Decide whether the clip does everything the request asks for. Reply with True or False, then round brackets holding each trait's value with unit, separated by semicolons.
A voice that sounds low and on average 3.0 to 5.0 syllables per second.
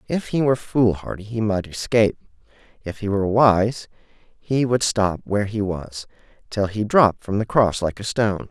True (105 Hz; 4.9 syllables/s)